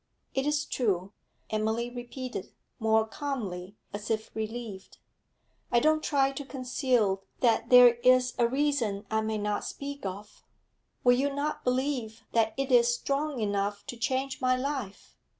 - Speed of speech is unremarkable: Yes, average, 150 wpm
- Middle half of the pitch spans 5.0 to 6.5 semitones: No, average, 3.7 semitones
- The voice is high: Yes, high, 240 Hz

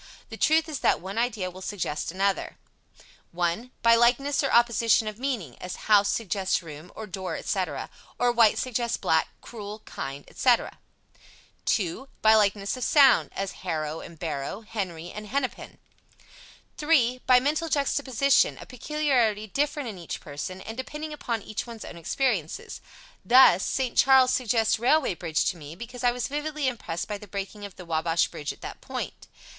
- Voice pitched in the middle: No, high, 220 Hz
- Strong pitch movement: Yes, wide, 5.7 semitones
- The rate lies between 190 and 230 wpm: No, average, 165 wpm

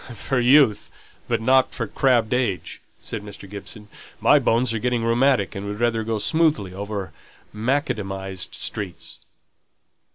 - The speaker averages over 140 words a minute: No, slow, 135 wpm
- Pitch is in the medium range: No, low, 115 Hz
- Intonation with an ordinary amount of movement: Yes, average, 3.6 semitones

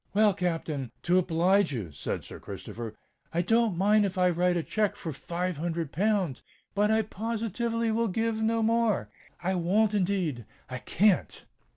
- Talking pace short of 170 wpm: Yes, average, 150 wpm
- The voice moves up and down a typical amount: Yes, average, 4.7 semitones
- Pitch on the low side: No, medium, 185 Hz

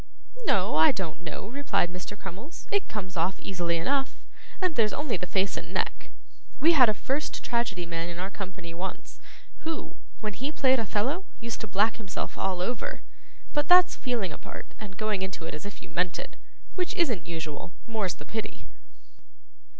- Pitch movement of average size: No, wide, 6.0 semitones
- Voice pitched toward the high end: Yes, high, 205 Hz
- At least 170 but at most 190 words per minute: Yes, average, 180 wpm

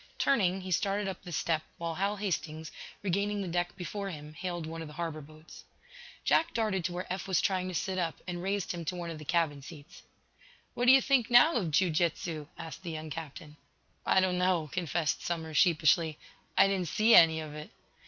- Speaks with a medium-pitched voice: Yes, medium, 175 Hz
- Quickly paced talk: Yes, fast, 210 wpm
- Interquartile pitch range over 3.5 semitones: No, average, 3.2 semitones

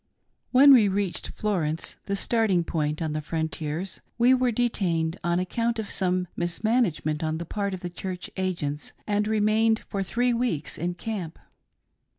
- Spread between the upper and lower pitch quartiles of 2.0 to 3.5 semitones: No, average, 5.1 semitones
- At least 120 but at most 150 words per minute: No, average, 170 wpm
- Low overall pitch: No, high, 190 Hz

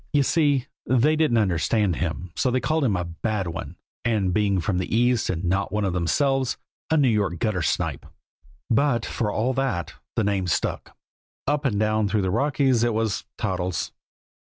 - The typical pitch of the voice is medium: No, low, 110 Hz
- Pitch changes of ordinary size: No, wide, 5.7 semitones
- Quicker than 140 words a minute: Yes, average, 185 wpm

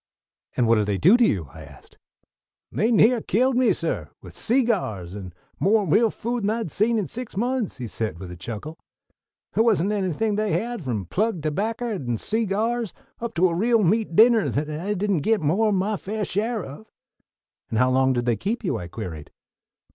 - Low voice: No, high, 200 Hz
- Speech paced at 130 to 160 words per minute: No, average, 200 wpm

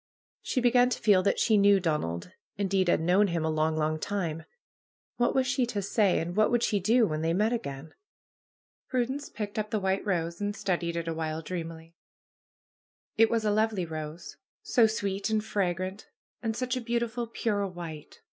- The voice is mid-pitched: No, high, 200 Hz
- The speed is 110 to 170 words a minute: No, average, 185 wpm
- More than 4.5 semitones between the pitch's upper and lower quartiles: Yes, average, 5.1 semitones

